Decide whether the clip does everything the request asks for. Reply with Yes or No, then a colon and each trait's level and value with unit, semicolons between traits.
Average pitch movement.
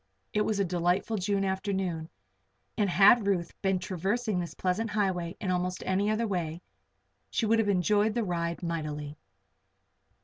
Yes: average, 3.0 semitones